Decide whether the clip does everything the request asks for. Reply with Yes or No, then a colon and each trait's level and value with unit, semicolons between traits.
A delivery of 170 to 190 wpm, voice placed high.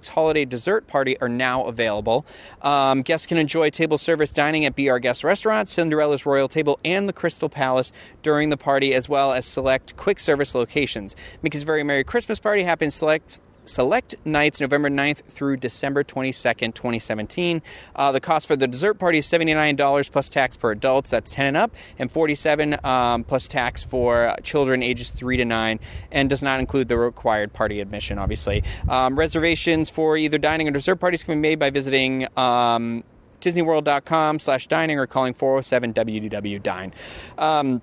No: average, 175 wpm; medium, 140 Hz